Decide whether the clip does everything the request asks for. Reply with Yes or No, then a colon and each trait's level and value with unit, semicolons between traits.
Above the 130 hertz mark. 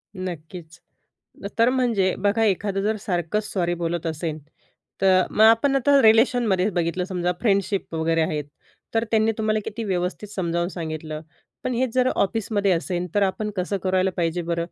Yes: high, 190 Hz